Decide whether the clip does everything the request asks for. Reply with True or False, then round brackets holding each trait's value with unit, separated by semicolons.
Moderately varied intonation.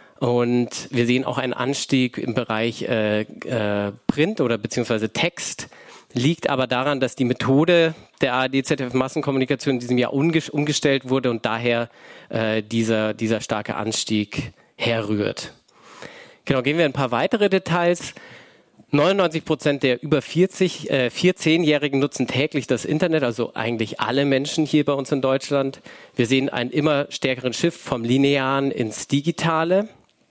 True (3.7 semitones)